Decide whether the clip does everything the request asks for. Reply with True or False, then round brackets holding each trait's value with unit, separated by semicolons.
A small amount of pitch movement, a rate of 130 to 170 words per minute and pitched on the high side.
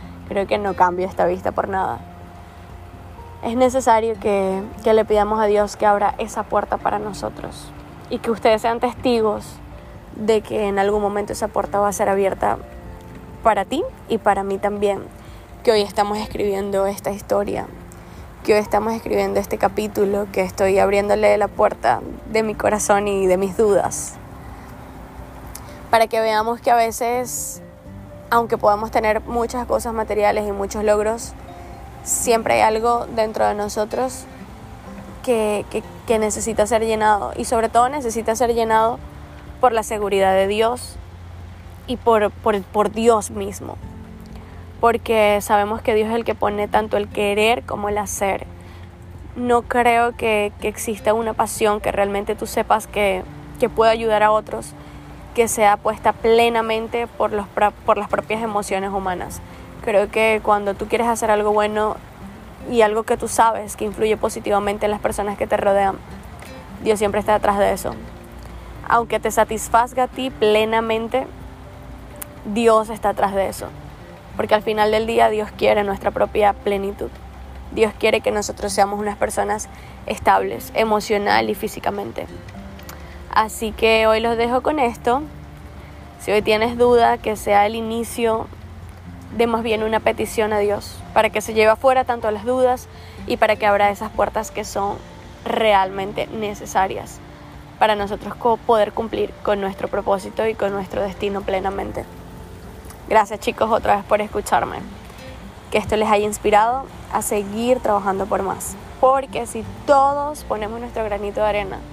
True (2.2 semitones; 155 wpm; 210 Hz)